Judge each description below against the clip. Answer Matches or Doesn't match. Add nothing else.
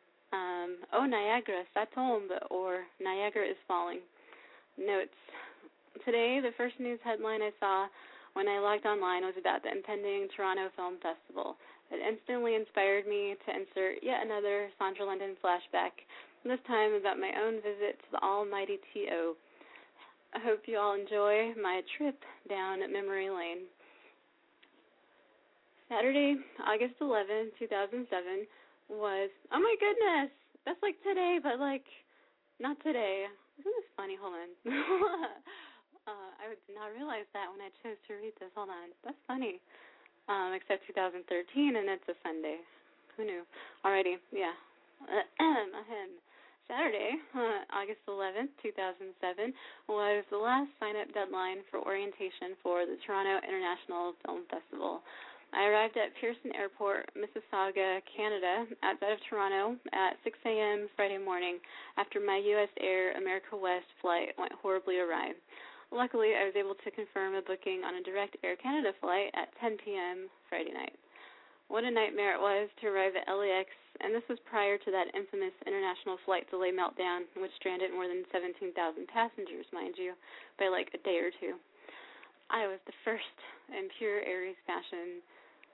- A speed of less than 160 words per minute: Matches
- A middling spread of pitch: Matches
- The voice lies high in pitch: Matches